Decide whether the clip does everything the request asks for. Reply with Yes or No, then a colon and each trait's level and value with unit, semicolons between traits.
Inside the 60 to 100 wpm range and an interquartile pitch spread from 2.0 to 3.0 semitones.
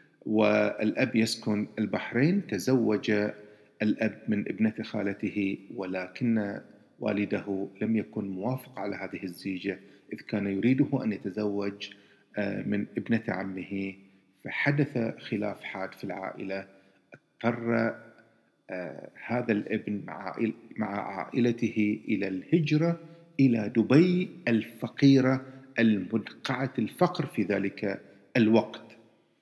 No: average, 90 wpm; average, 3.5 semitones